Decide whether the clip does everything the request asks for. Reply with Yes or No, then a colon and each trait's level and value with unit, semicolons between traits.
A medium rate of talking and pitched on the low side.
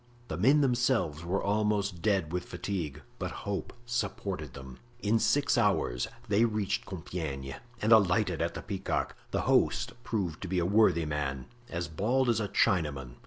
Yes: average, 165 wpm; very low, 95 Hz